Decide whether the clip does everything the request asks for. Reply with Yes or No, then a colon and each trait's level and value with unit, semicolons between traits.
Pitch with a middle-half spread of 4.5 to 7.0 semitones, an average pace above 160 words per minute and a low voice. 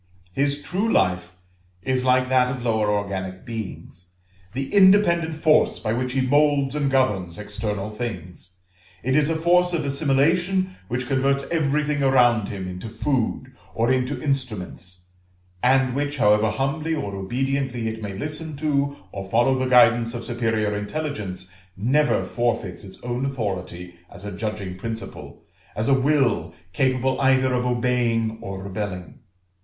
No: average, 5.0 semitones; average, 145 wpm; low, 125 Hz